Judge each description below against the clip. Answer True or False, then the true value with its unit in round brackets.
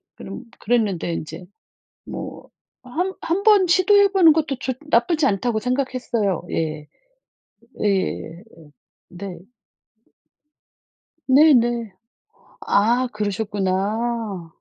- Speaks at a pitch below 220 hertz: False (230 Hz)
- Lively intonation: True (6.2 semitones)